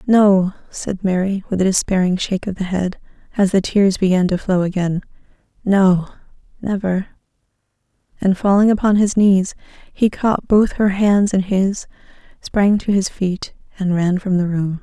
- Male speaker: No, female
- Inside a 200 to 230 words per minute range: No, average, 160 wpm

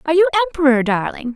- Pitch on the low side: No, very high, 265 Hz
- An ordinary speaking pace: Yes, average, 175 wpm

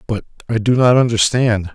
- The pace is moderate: Yes, average, 170 wpm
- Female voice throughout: No, male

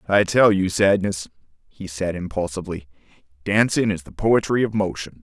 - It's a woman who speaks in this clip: No, male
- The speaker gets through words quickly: No, average, 150 wpm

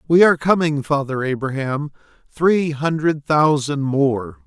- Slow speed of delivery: Yes, slow, 120 wpm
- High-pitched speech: No, medium, 150 Hz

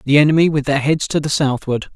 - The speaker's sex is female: No, male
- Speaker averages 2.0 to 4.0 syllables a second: No, 6.2 syllables/s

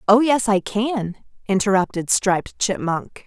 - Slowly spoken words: Yes, slow, 130 wpm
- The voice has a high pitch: Yes, high, 205 Hz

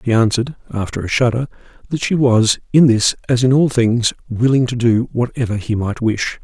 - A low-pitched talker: Yes, low, 120 Hz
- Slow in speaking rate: No, average, 175 wpm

